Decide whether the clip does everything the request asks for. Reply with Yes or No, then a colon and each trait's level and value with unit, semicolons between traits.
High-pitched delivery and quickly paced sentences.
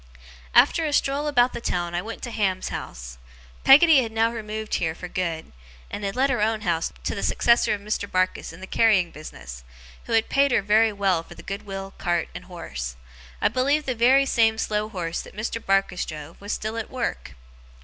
Yes: high, 210 Hz; fast, 210 wpm